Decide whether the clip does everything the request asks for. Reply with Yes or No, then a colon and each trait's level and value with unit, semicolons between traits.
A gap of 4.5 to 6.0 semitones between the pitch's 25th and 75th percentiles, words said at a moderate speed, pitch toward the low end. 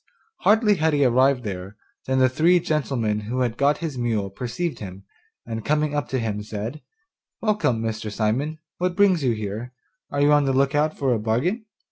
Yes: wide, 5.4 semitones; average, 190 wpm; low, 130 Hz